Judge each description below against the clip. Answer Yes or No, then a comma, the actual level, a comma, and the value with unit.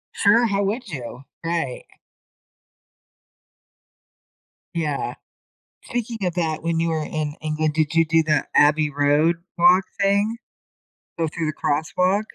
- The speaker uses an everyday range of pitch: Yes, average, 4.1 semitones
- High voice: No, medium, 165 Hz